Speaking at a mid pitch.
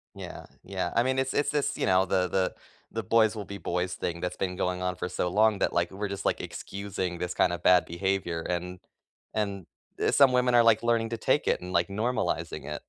No: very low, 95 Hz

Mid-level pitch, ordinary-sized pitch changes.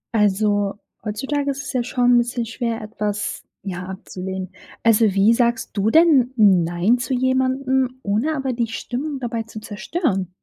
No: high, 230 Hz; average, 4.0 semitones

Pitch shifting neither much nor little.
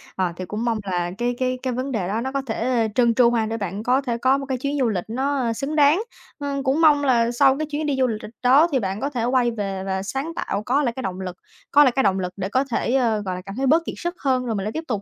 Yes: average, 4.3 semitones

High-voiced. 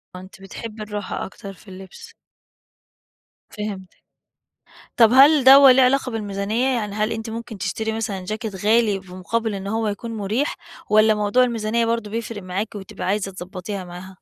Yes: high, 215 Hz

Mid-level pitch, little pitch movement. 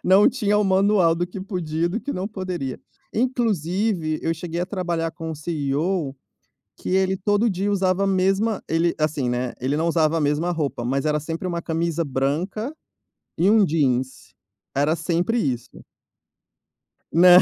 No: medium, 170 Hz; average, 3.9 semitones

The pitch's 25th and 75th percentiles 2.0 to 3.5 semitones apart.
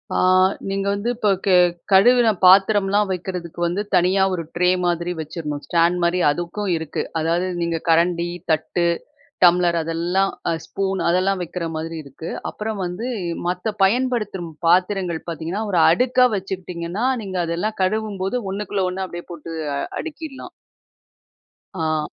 Yes: average, 2.8 semitones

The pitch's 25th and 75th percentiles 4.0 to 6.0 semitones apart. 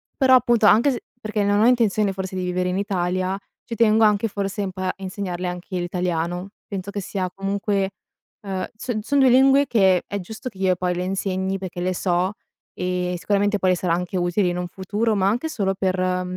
No: narrow, 2.4 semitones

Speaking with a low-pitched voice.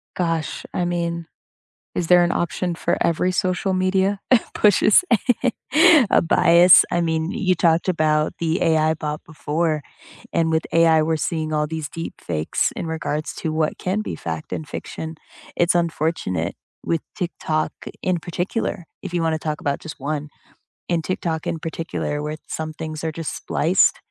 No: medium, 165 Hz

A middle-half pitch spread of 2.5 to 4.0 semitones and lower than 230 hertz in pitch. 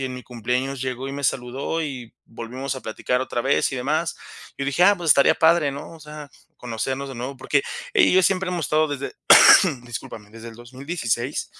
Yes: average, 3.5 semitones; low, 135 Hz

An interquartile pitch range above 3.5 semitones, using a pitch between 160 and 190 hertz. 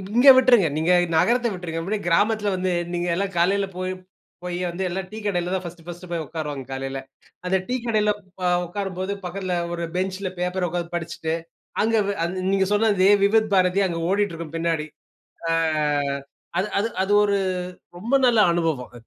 No: average, 3.0 semitones; medium, 185 Hz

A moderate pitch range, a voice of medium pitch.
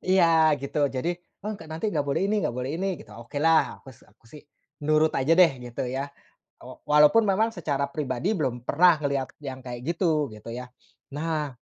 Yes: average, 4.0 semitones; medium, 150 Hz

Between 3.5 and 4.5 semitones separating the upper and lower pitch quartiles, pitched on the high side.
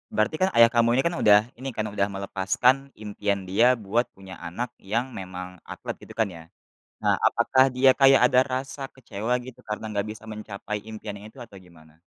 No: average, 3.9 semitones; low, 110 Hz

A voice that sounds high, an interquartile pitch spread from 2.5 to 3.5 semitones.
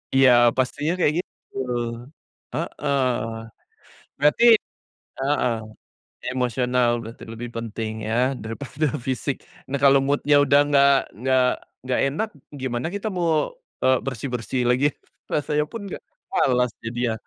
No: low, 130 Hz; average, 3.0 semitones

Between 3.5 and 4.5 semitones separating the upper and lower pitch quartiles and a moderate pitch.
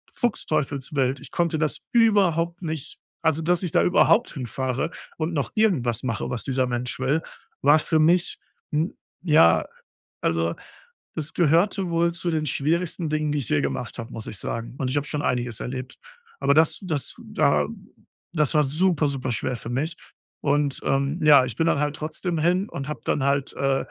Yes: average, 4.1 semitones; medium, 150 Hz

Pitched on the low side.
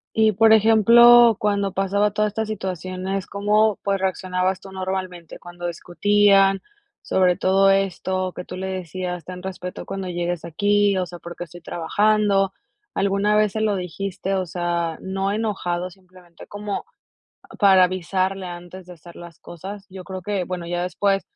No: high, 190 Hz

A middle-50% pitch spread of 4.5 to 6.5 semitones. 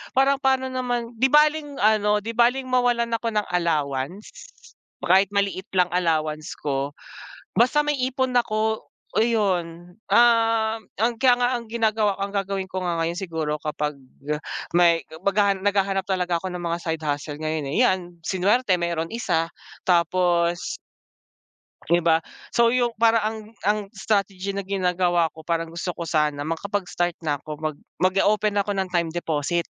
Yes: average, 4.8 semitones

